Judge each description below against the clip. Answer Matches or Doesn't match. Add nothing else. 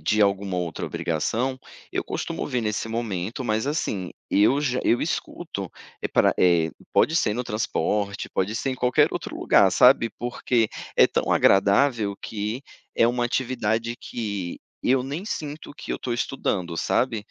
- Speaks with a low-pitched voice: Matches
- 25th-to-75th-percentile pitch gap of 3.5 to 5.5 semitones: Matches